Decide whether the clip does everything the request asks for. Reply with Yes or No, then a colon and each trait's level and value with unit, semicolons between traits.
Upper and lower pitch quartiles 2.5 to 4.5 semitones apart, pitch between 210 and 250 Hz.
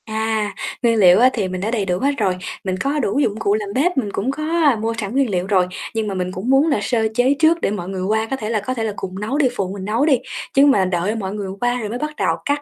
No: average, 5.1 semitones; high, 220 Hz